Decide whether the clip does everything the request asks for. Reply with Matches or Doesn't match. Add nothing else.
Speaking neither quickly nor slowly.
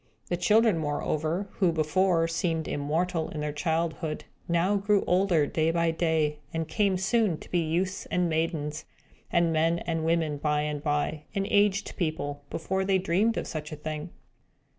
Matches